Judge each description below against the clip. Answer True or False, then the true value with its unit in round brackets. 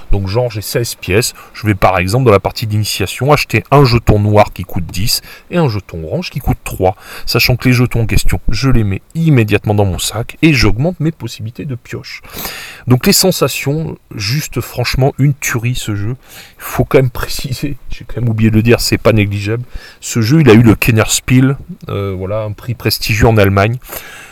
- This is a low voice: True (115 Hz)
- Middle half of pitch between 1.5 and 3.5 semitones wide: False (3.9 semitones)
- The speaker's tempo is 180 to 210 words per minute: True (205 wpm)